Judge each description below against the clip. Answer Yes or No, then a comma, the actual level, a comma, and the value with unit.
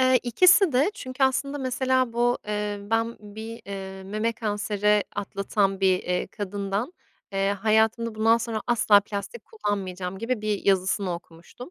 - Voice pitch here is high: Yes, high, 215 Hz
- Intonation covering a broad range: No, average, 3.4 semitones